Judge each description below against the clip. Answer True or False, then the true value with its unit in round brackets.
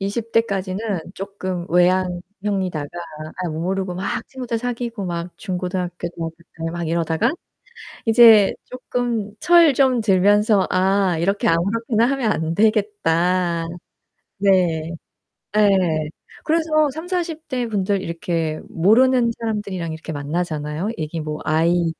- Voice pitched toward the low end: False (190 Hz)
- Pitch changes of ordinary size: True (4.9 semitones)